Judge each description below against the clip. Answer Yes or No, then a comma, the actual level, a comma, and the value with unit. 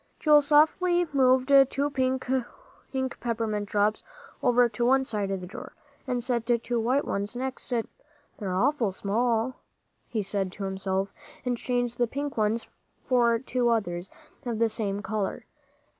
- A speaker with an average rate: Yes, average, 155 wpm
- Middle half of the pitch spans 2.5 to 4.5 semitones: Yes, average, 3.8 semitones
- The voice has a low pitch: No, high, 240 Hz